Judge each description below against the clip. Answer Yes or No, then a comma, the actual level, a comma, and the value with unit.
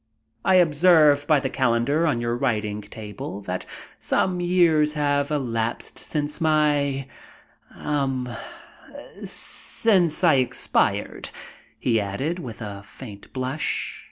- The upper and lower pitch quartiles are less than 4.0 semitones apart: No, average, 4.7 semitones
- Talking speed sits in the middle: No, slow, 110 wpm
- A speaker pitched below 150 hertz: Yes, medium, 140 Hz